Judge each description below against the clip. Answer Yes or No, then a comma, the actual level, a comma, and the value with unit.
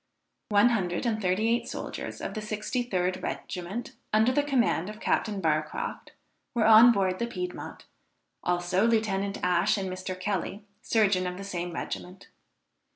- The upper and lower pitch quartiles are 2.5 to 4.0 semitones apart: Yes, average, 3.4 semitones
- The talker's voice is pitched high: Yes, high, 200 Hz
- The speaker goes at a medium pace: Yes, average, 150 wpm